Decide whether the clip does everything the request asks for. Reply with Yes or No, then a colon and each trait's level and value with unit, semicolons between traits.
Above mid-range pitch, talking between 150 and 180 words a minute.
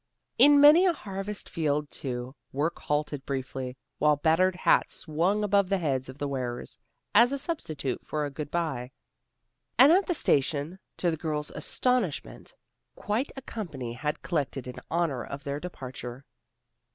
No: medium, 150 Hz; average, 155 wpm